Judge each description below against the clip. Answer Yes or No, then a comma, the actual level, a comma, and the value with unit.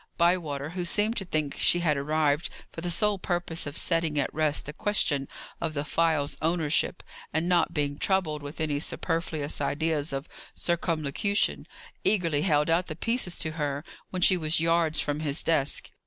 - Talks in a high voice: No, medium, 160 Hz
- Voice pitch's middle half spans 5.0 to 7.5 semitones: No, average, 2.8 semitones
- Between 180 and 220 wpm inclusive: No, average, 170 wpm